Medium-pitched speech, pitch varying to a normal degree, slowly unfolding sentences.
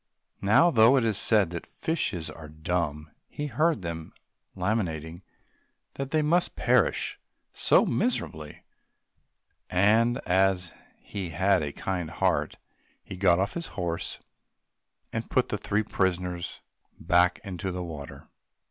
No: very low, 95 Hz; average, 4.7 semitones; slow, 130 wpm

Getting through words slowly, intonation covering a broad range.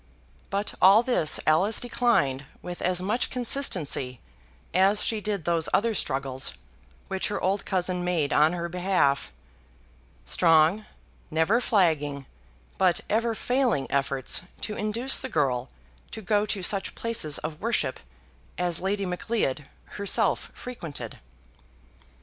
Yes: slow, 125 wpm; wide, 5.8 semitones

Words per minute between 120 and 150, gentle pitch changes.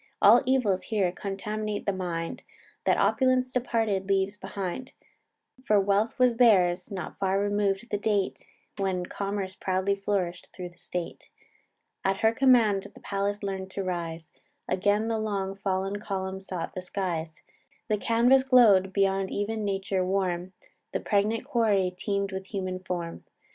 Yes: average, 145 wpm; narrow, 2.2 semitones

